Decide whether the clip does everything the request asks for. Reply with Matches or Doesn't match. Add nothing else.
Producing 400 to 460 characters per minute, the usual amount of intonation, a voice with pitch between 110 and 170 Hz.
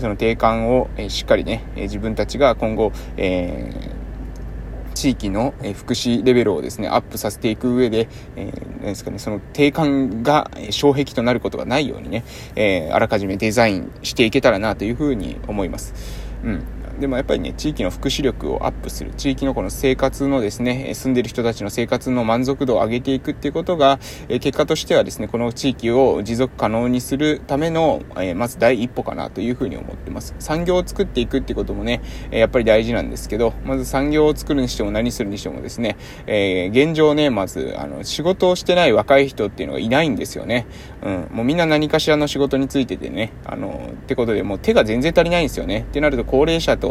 Matches